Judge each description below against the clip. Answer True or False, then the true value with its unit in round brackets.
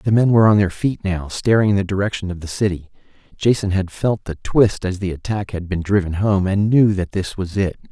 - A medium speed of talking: False (245 wpm)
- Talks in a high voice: False (95 Hz)